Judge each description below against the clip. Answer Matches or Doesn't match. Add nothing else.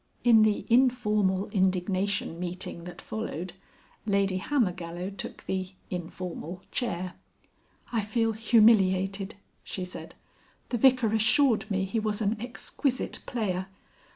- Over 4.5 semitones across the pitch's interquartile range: Doesn't match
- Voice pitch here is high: Matches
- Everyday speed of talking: Doesn't match